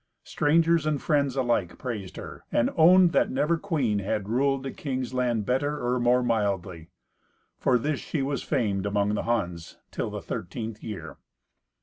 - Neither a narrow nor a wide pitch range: No, wide, 5.7 semitones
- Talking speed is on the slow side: No, average, 160 wpm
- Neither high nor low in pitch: No, low, 125 Hz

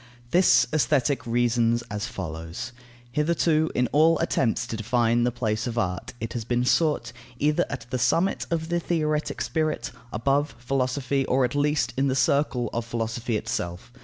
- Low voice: Yes, low, 125 Hz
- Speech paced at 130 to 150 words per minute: No, average, 160 wpm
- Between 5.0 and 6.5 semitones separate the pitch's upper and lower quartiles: No, average, 4.2 semitones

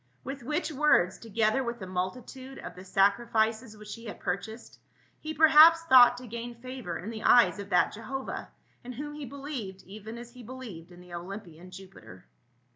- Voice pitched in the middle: No, high, 230 Hz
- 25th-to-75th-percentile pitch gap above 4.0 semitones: Yes, average, 5.0 semitones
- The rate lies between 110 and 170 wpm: No, average, 190 wpm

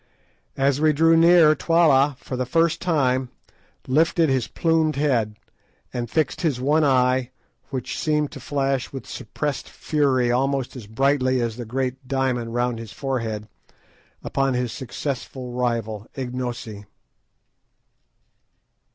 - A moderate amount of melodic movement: Yes, average, 3.1 semitones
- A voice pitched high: No, low, 130 Hz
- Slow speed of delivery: Yes, slow, 125 wpm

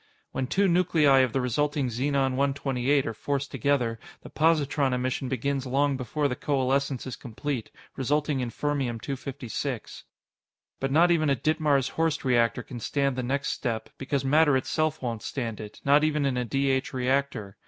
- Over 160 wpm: Yes, average, 170 wpm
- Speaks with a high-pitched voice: No, low, 135 Hz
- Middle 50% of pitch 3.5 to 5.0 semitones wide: No, narrow, 2.4 semitones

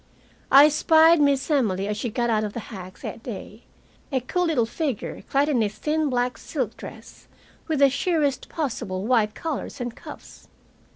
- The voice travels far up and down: Yes, wide, 5.7 semitones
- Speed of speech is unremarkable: Yes, average, 175 wpm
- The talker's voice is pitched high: Yes, very high, 255 Hz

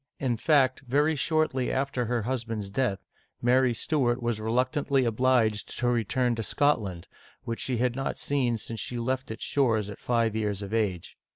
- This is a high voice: No, low, 120 Hz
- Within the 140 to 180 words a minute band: Yes, average, 170 wpm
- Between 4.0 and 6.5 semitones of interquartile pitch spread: No, average, 2.9 semitones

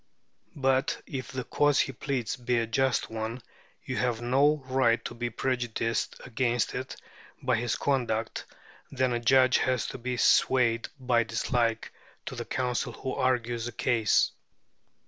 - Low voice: Yes, low, 125 Hz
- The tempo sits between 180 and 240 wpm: No, average, 155 wpm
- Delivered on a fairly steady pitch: Yes, narrow, 2.0 semitones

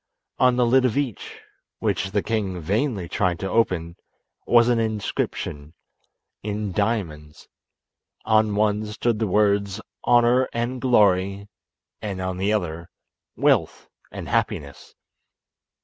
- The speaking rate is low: Yes, slow, 120 wpm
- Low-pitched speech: Yes, low, 105 Hz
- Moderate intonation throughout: Yes, average, 3.8 semitones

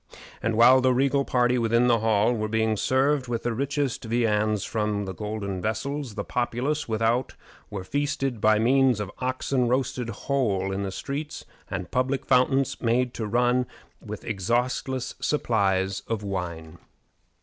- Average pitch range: Yes, average, 3.5 semitones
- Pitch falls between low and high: No, low, 120 Hz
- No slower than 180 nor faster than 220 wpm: No, average, 150 wpm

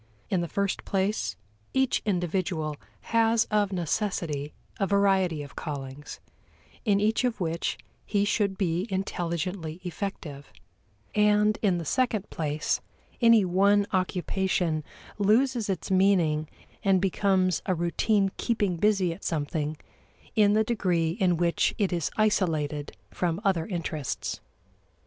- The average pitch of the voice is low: No, high, 190 Hz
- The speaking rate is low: Yes, slow, 125 wpm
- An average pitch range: Yes, average, 3.7 semitones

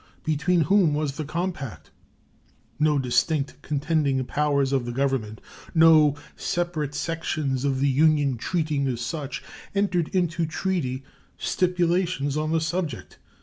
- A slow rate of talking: Yes, slow, 125 wpm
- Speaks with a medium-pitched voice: Yes, medium, 150 Hz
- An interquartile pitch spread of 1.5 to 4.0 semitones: Yes, average, 3.4 semitones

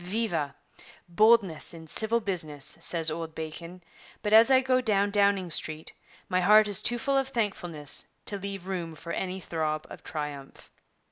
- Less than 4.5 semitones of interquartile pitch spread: No, average, 4.8 semitones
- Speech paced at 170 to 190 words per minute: No, average, 160 wpm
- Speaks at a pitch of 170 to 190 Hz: Yes, medium, 185 Hz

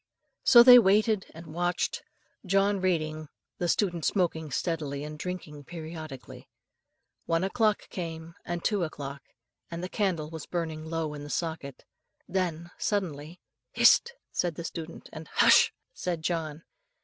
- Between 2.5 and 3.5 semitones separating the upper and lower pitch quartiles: Yes, average, 2.9 semitones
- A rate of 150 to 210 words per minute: No, slow, 135 wpm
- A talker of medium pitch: Yes, medium, 165 Hz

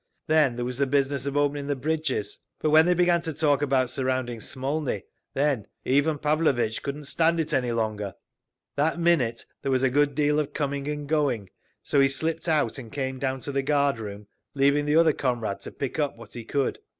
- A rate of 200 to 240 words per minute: Yes, fast, 205 wpm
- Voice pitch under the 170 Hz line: Yes, medium, 140 Hz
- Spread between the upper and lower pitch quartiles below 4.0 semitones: Yes, average, 2.7 semitones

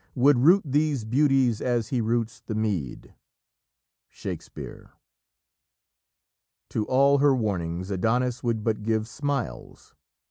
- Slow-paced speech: Yes, slow, 110 wpm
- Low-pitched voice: Yes, low, 120 Hz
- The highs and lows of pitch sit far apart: No, average, 3.8 semitones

